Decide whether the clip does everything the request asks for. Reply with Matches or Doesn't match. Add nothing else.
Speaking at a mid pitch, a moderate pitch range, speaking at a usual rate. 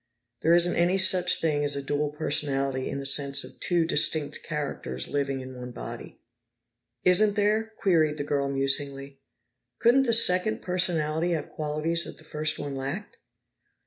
Matches